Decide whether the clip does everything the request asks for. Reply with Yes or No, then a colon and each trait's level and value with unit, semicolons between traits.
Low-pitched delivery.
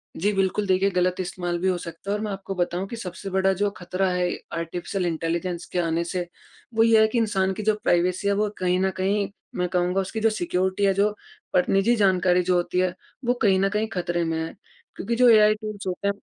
No: high, 190 Hz